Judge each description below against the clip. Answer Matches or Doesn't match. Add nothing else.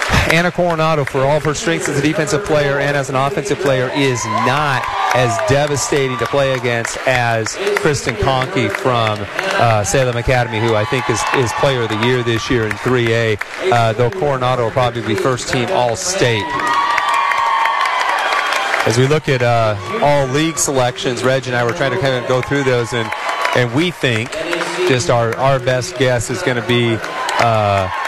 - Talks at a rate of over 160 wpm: Matches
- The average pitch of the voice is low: Matches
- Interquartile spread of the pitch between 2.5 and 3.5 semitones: Matches